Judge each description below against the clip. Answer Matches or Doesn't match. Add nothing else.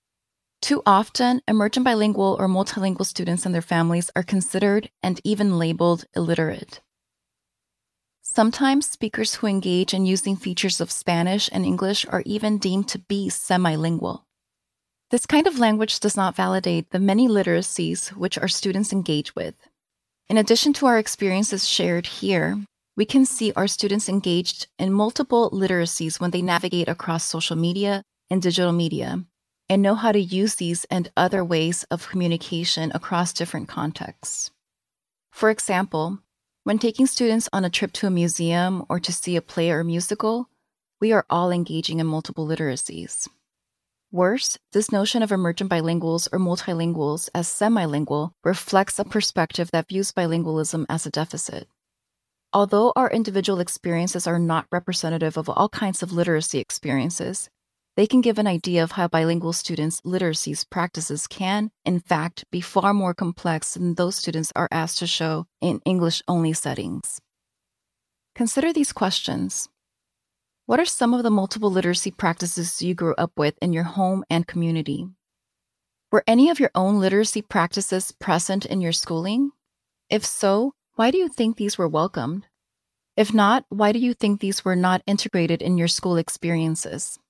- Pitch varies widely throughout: Doesn't match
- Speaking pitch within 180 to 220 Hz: Matches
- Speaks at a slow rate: Doesn't match